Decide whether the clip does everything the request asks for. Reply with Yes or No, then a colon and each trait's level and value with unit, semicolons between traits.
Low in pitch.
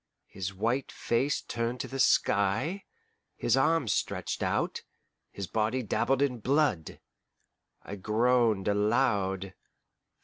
Yes: low, 115 Hz